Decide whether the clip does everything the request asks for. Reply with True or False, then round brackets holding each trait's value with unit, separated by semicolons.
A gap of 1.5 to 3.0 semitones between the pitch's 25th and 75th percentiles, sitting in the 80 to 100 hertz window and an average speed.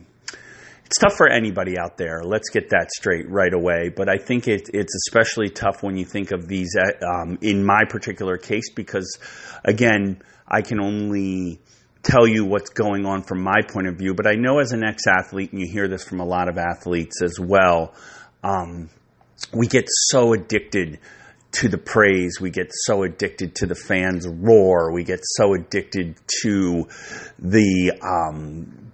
True (2.7 semitones; 95 Hz; 175 wpm)